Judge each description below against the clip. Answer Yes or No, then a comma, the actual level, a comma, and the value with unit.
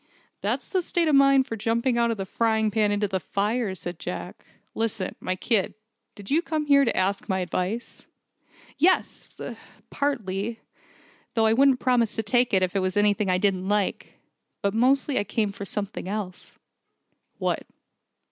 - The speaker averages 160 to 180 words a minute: Yes, average, 175 wpm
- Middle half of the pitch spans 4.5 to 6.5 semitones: No, average, 4.0 semitones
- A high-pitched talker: Yes, high, 215 Hz